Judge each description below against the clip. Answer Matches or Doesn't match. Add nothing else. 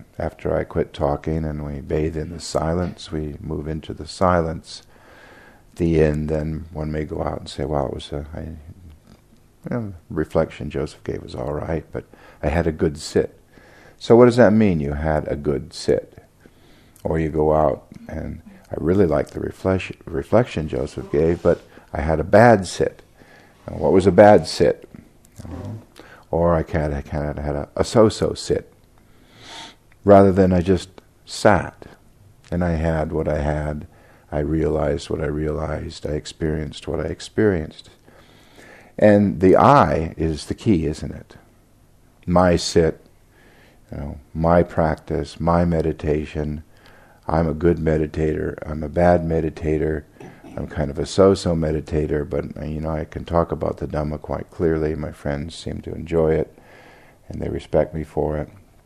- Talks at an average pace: Matches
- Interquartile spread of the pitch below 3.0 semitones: Matches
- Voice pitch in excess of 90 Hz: Doesn't match